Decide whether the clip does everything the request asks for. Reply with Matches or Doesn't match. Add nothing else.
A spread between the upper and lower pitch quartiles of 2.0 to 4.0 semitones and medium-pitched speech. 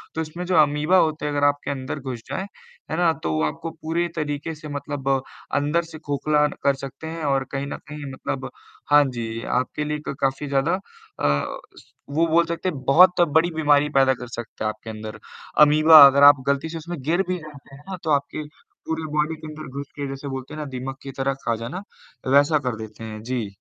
Matches